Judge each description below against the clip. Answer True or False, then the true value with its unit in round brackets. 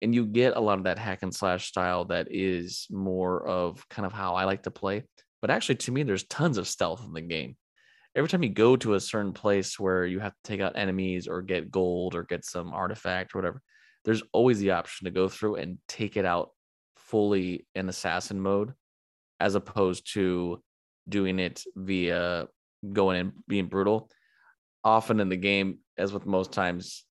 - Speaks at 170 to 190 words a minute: False (200 wpm)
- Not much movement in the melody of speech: True (2.1 semitones)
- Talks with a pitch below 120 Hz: True (95 Hz)